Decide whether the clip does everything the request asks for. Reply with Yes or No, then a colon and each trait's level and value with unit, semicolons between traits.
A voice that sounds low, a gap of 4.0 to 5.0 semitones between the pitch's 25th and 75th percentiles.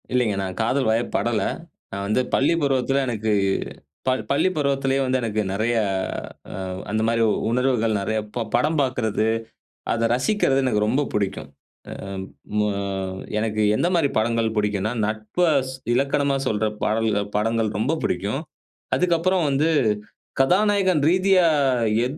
Yes: low, 120 Hz; average, 4.5 semitones